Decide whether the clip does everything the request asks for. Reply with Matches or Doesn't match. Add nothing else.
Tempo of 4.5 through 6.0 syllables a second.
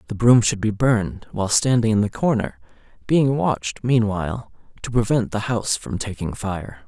Matches